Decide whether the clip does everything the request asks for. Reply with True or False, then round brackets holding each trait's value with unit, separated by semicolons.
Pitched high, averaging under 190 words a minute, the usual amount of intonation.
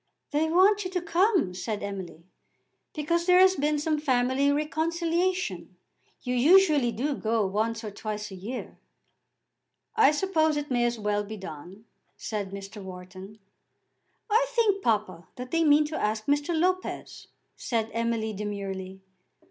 False (250 Hz; 145 wpm; 7.9 semitones)